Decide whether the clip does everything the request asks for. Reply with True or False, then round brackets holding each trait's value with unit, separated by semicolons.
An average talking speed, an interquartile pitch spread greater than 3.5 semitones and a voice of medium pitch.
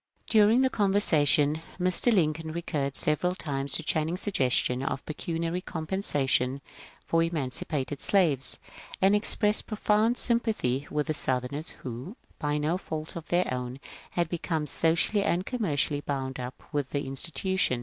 True (145 wpm; 5.0 semitones; 160 Hz)